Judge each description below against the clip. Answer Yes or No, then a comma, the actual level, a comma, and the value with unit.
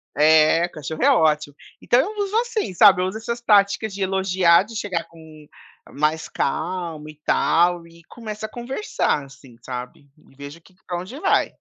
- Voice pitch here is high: No, medium, 175 Hz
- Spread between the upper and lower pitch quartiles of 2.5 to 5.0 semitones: No, wide, 5.6 semitones